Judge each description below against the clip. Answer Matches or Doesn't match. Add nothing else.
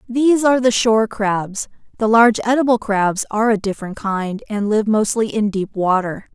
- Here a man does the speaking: Doesn't match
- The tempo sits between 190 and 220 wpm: Doesn't match